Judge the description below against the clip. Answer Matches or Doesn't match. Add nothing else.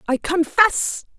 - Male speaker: Doesn't match